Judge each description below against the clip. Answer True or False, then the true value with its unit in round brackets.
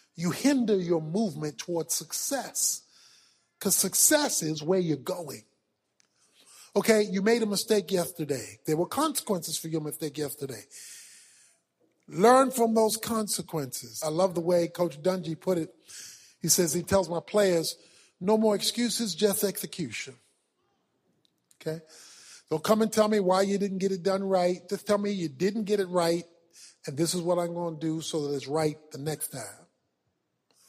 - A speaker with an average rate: True (165 wpm)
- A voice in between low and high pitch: True (180 Hz)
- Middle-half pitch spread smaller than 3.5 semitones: False (4.1 semitones)